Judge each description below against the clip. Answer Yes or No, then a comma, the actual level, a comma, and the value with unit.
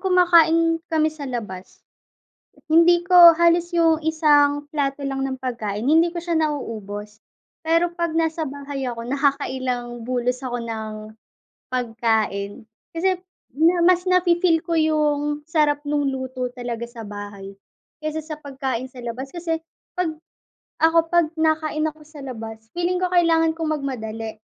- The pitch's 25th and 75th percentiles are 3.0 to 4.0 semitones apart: No, average, 5.1 semitones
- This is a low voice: No, very high, 290 Hz